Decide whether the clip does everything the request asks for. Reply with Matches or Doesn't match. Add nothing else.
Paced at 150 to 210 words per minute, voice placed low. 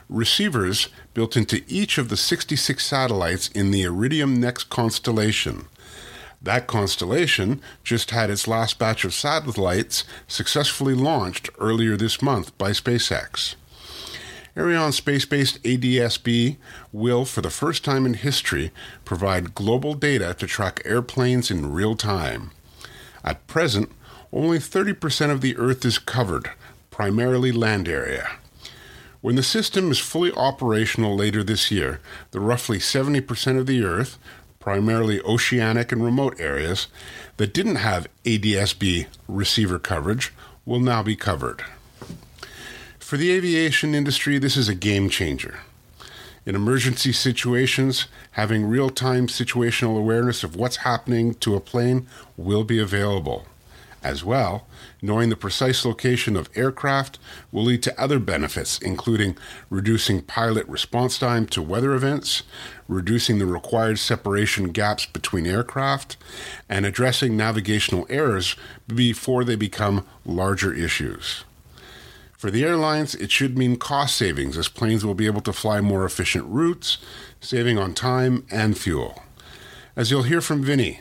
Doesn't match